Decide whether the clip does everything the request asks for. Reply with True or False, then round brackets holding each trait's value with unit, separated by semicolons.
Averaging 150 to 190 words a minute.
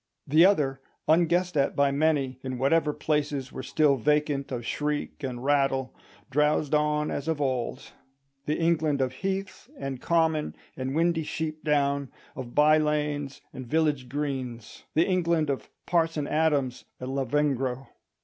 False (140 wpm)